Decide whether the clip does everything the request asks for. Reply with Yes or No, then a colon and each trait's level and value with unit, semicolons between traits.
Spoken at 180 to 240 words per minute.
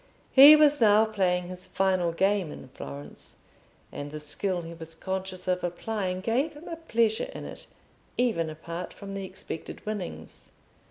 No: average, 160 wpm